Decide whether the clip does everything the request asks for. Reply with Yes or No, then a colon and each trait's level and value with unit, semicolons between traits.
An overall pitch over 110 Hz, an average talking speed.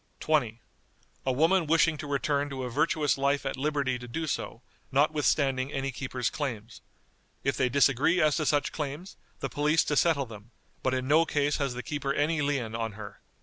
Yes: medium, 140 Hz; average, 190 wpm